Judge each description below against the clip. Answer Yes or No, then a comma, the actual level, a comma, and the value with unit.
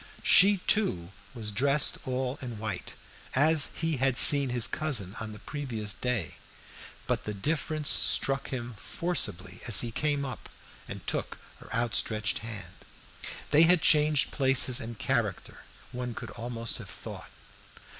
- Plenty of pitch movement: No, average, 4.9 semitones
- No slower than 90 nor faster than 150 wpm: Yes, average, 145 wpm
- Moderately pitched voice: No, low, 125 Hz